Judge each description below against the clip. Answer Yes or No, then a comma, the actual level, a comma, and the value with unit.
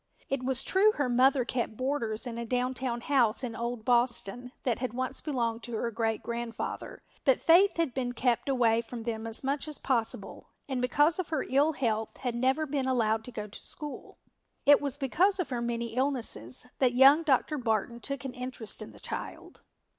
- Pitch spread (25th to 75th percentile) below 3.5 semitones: Yes, average, 2.8 semitones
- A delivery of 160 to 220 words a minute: Yes, average, 195 wpm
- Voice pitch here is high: Yes, very high, 250 Hz